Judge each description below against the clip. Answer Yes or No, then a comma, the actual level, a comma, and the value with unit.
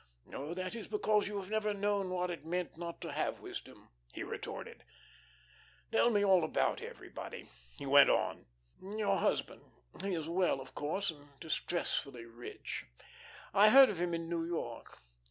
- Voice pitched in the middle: Yes, medium, 180 Hz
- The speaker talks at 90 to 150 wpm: No, average, 160 wpm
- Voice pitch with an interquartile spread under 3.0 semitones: No, average, 4.1 semitones